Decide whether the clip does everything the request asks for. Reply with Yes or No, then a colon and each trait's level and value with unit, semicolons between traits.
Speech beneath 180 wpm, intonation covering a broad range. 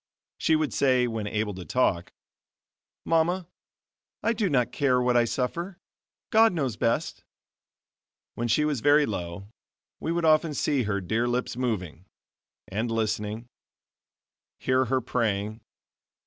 Yes: slow, 135 wpm; wide, 5.8 semitones